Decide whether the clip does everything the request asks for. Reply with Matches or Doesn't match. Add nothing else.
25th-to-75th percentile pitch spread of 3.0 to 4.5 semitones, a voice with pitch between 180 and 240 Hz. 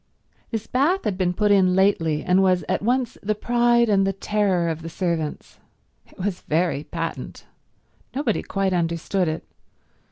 Matches